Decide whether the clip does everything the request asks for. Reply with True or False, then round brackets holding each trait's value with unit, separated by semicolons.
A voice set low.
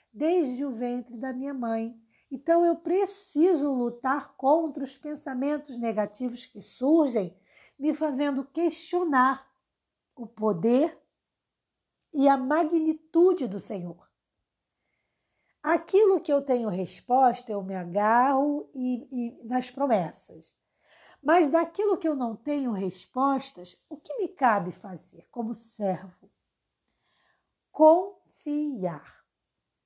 False (265 Hz)